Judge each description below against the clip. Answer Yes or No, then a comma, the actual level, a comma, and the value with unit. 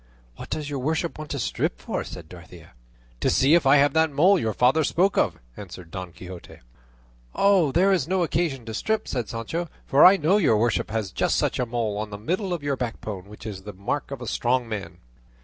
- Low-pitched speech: Yes, low, 130 Hz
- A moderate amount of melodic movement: No, wide, 7.4 semitones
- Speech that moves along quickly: Yes, fast, 220 wpm